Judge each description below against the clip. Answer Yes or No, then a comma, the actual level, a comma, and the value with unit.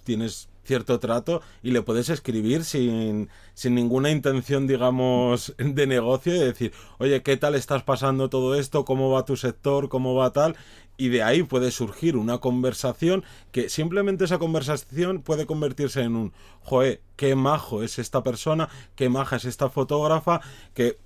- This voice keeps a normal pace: Yes, average, 160 wpm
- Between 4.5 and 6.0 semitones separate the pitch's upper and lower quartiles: No, average, 2.9 semitones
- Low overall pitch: Yes, low, 130 Hz